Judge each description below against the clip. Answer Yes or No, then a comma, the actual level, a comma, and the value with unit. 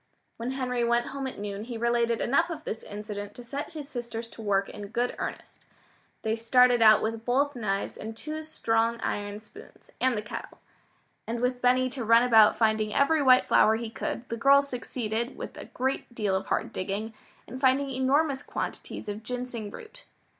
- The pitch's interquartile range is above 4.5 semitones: No, average, 3.1 semitones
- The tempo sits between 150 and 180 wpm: No, average, 190 wpm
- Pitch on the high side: Yes, high, 235 Hz